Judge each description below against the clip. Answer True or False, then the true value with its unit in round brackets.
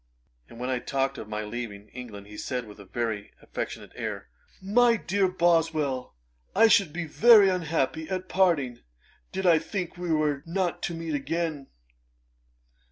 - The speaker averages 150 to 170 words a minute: True (160 wpm)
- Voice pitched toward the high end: False (160 Hz)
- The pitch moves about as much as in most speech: False (6.4 semitones)